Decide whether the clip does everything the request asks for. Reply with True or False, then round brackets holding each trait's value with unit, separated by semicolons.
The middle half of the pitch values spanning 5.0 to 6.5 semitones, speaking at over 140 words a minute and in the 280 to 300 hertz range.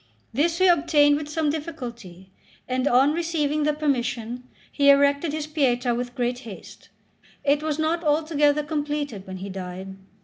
False (3.9 semitones; 150 wpm; 290 Hz)